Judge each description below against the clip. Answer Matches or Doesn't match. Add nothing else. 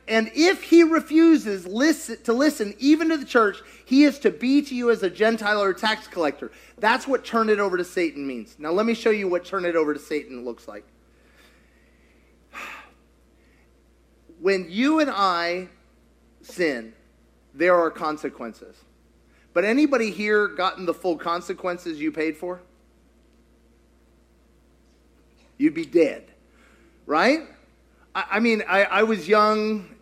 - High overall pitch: Matches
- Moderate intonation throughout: Doesn't match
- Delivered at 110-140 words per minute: Doesn't match